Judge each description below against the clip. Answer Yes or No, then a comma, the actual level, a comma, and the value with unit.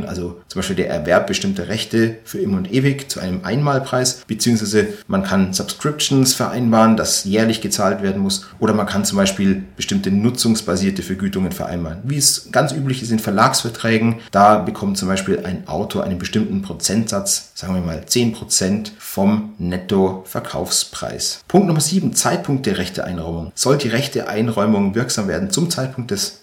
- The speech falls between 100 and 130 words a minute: No, average, 155 wpm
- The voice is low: Yes, low, 115 Hz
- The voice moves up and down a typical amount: No, wide, 7.2 semitones